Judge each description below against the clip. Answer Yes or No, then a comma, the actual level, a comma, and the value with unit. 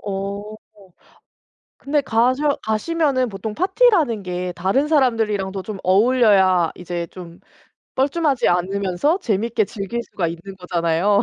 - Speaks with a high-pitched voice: Yes, high, 210 Hz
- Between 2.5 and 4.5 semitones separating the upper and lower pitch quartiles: No, wide, 5.6 semitones